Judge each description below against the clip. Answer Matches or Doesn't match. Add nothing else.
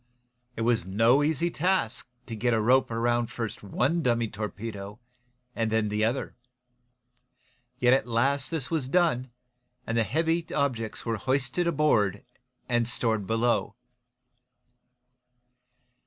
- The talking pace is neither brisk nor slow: Doesn't match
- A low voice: Matches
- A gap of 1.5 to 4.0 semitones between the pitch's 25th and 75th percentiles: Matches